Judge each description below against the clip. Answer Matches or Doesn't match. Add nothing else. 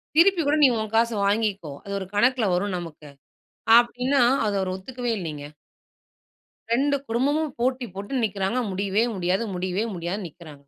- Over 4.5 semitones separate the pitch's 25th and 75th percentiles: Matches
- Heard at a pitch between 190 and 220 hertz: Matches